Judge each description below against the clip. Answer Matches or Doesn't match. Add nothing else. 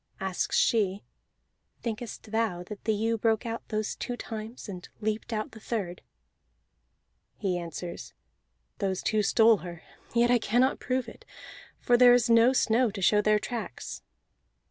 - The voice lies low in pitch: Doesn't match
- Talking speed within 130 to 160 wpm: Matches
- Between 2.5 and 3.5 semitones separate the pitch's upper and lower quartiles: Matches